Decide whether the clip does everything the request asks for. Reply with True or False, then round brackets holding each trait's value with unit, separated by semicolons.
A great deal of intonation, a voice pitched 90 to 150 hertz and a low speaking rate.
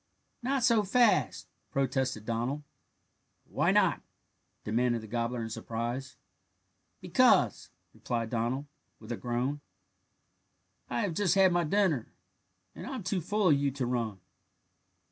True (7.8 semitones; 135 Hz; 125 wpm)